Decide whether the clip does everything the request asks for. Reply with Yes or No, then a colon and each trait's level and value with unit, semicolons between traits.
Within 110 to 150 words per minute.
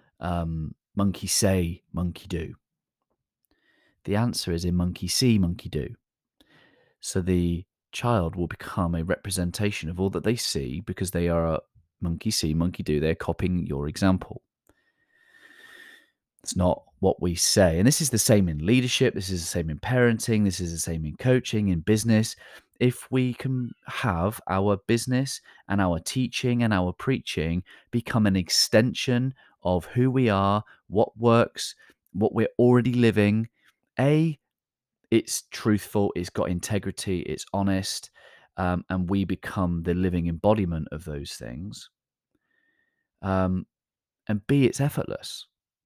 Yes: average, 145 wpm